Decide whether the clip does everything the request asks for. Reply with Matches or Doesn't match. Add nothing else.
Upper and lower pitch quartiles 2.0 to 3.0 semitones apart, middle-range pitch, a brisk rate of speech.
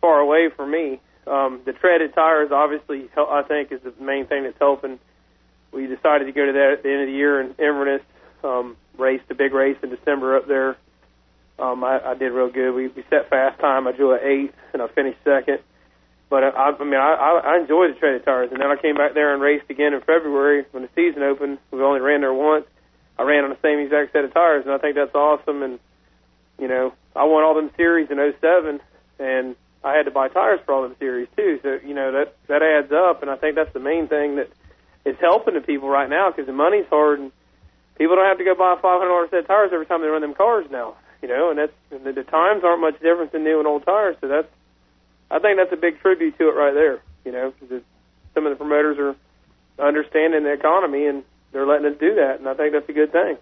Matches